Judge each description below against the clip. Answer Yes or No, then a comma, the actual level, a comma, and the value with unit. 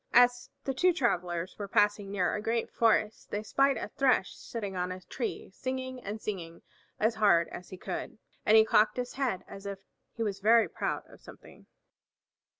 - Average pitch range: Yes, average, 4.1 semitones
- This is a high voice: Yes, high, 215 Hz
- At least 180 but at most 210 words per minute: Yes, average, 185 wpm